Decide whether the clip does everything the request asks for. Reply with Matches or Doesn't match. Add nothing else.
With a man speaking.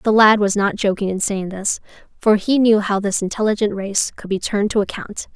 Doesn't match